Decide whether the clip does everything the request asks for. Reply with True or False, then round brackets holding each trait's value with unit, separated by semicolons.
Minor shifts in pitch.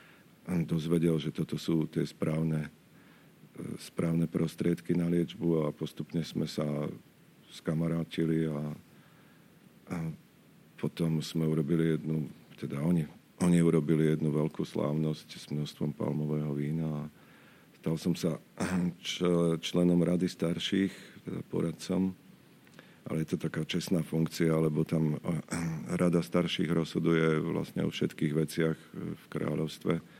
True (1.5 semitones)